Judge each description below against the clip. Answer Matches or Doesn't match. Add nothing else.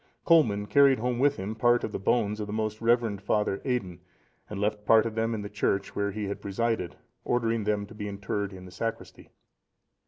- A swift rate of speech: Matches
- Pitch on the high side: Doesn't match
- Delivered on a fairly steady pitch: Matches